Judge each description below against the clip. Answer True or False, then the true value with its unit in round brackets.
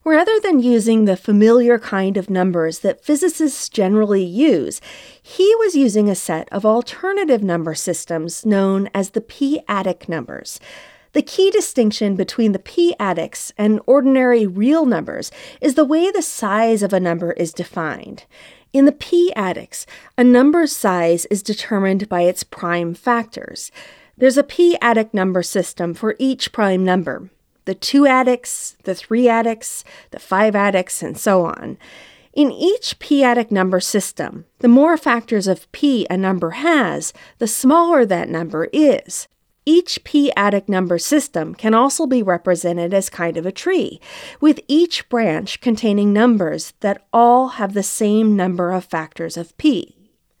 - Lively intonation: True (6.7 semitones)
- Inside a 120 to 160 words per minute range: True (150 wpm)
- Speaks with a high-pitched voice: True (220 Hz)